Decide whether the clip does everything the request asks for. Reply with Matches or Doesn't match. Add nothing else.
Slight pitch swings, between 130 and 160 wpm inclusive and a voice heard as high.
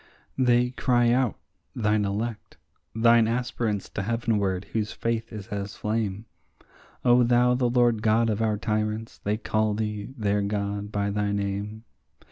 Doesn't match